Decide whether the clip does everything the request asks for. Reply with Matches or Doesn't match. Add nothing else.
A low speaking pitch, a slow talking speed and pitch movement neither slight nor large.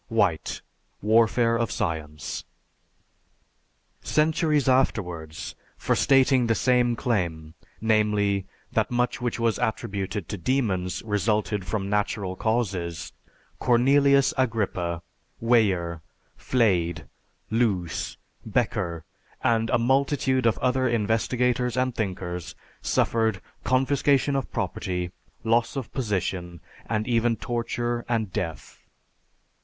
Matches